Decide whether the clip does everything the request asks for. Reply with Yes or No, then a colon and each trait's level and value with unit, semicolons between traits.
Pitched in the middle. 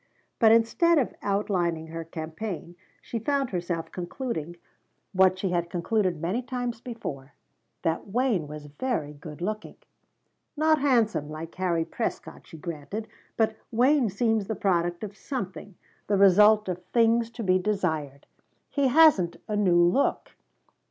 No: high, 195 Hz